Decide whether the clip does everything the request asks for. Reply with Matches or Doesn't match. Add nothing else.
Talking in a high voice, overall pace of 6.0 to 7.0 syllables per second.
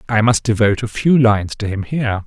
Doesn't match